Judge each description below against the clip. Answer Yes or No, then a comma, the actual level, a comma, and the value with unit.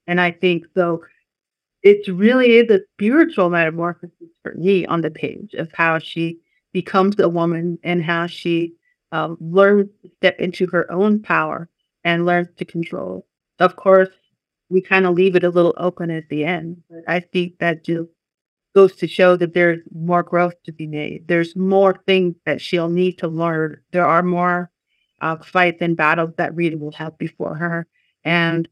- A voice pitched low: No, medium, 175 Hz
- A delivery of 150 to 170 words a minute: No, average, 180 wpm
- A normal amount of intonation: No, narrow, 1.7 semitones